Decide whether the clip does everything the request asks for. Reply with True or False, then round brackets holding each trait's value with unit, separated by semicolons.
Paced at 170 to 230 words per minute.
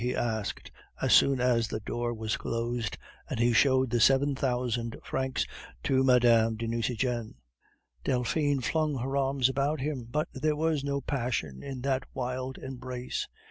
False (155 wpm)